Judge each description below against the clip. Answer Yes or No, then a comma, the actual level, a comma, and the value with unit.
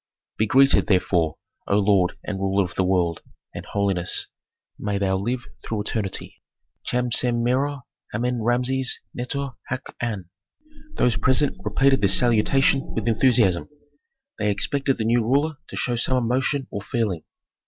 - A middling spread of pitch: Yes, average, 4.5 semitones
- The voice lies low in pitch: Yes, low, 115 Hz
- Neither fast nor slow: Yes, average, 145 wpm